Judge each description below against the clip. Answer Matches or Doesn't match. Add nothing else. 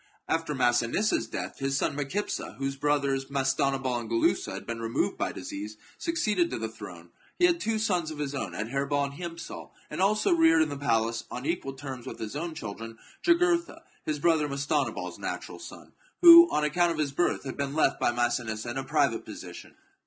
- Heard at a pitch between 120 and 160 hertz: Matches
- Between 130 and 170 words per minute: Doesn't match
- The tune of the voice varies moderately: Doesn't match